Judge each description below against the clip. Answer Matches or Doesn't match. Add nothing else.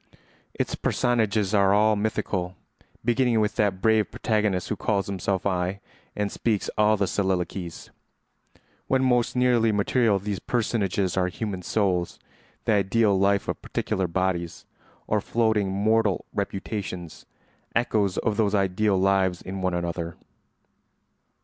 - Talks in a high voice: Doesn't match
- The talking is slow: Matches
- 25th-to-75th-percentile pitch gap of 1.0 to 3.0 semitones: Matches